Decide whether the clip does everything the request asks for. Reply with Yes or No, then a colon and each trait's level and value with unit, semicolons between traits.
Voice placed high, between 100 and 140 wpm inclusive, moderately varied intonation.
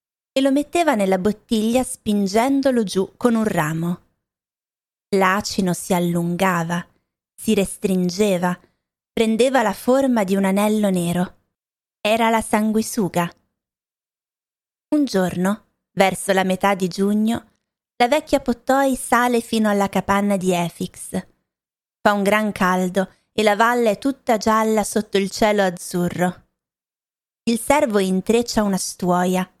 Yes: high, 205 Hz; average, 120 wpm; average, 3.7 semitones